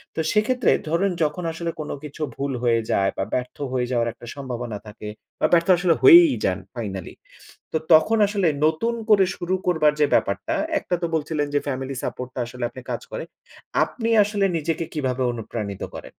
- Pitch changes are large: Yes, wide, 6.4 semitones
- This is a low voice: No, medium, 150 Hz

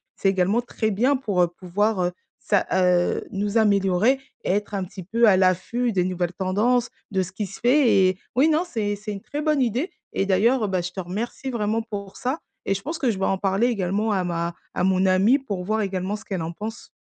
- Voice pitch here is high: Yes, high, 200 Hz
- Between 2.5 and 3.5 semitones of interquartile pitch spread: No, average, 3.9 semitones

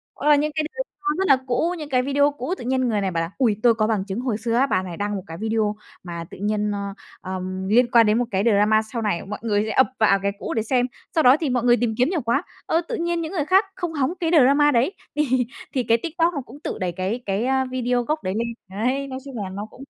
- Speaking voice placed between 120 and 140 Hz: No, high, 240 Hz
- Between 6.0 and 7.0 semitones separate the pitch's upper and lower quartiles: No, average, 5.2 semitones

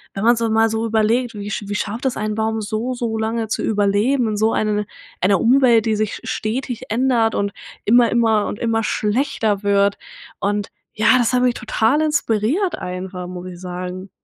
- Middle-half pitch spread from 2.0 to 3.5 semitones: Yes, narrow, 2.4 semitones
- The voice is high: Yes, high, 220 Hz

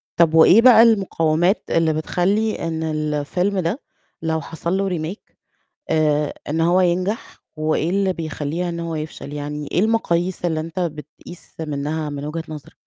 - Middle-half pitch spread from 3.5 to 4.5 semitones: No, average, 2.9 semitones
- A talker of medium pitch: Yes, medium, 165 Hz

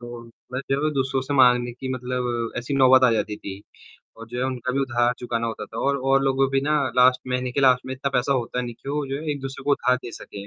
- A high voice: No, low, 125 Hz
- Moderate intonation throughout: No, narrow, 1.9 semitones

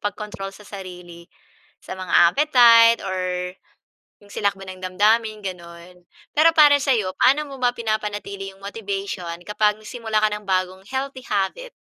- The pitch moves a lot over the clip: No, average, 3.7 semitones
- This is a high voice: Yes, high, 205 Hz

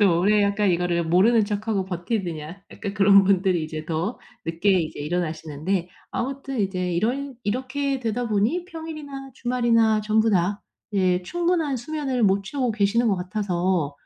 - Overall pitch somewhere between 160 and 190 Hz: No, high, 205 Hz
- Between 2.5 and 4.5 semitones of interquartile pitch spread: No, average, 5.3 semitones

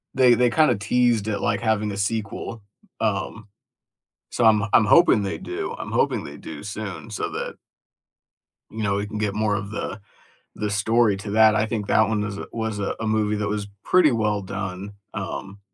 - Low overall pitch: Yes, low, 105 Hz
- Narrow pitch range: Yes, narrow, 2.0 semitones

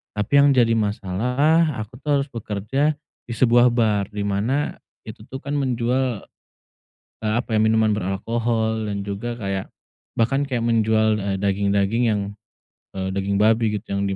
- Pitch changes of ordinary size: Yes, average, 3.2 semitones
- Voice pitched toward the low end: Yes, low, 110 Hz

